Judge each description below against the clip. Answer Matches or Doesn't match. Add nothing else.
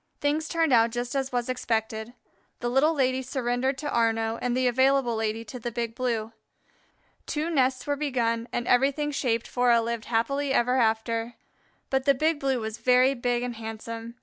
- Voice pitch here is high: Matches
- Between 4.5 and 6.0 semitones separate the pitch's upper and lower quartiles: Doesn't match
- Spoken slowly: Doesn't match